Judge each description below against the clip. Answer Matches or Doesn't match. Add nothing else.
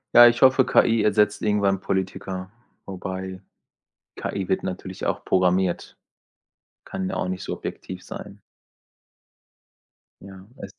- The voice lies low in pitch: Matches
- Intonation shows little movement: Matches